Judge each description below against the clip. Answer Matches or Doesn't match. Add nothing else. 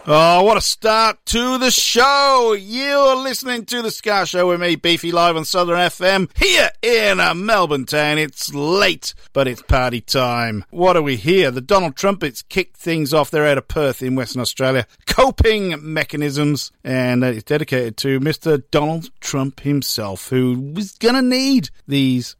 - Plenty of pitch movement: Matches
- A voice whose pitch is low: Doesn't match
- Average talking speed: Matches